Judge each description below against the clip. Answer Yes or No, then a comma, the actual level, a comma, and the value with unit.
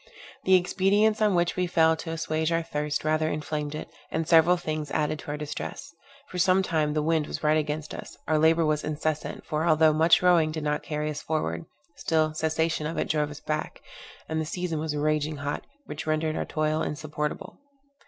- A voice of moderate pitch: Yes, medium, 155 Hz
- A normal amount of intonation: No, narrow, 1.4 semitones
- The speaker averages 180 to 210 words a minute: Yes, average, 200 wpm